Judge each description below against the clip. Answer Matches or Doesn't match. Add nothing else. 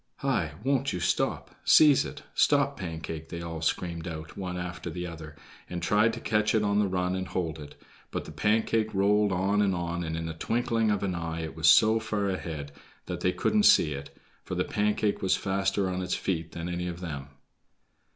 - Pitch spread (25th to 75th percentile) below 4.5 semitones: Matches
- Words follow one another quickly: Matches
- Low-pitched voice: Matches